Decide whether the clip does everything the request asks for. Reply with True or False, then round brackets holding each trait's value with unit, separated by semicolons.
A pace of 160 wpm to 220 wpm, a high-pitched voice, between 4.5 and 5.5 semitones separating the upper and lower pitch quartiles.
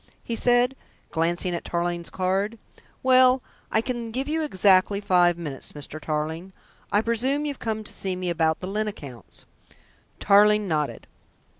False (150 wpm; 195 Hz; 5.2 semitones)